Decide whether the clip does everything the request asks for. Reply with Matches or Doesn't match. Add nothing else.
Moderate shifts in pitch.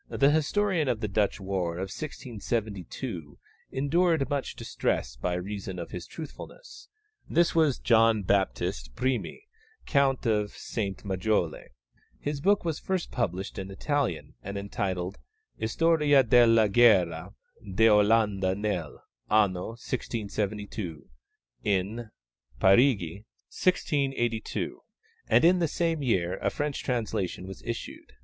Doesn't match